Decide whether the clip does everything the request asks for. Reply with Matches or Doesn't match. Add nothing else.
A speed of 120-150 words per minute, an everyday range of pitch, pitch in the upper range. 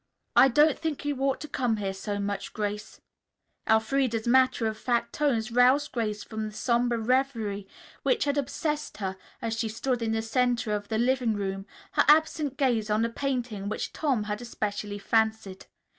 Doesn't match